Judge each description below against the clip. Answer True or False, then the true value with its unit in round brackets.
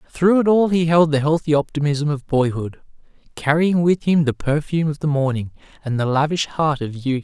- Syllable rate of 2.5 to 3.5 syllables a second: False (5.3 syllables/s)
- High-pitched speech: False (150 Hz)